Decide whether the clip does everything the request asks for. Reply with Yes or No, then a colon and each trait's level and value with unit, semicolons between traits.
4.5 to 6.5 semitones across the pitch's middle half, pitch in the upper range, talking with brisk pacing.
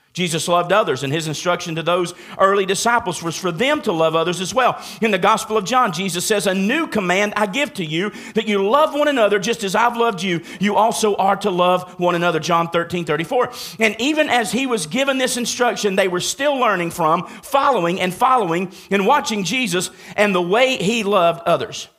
Yes: average, 4.9 semitones; high, 200 Hz; fast, 210 wpm